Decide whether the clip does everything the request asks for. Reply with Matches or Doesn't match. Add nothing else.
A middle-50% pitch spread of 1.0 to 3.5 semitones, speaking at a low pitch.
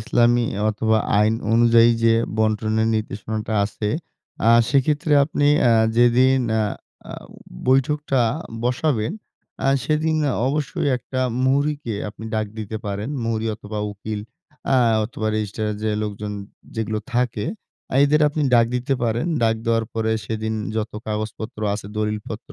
Matches